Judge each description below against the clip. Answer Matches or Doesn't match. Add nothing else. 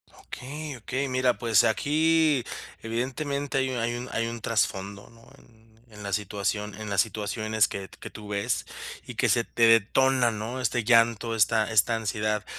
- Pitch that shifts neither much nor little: Matches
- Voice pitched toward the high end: Doesn't match